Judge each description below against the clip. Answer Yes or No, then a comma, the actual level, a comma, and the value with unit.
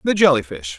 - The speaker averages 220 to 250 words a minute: Yes, fast, 230 wpm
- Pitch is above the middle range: No, low, 130 Hz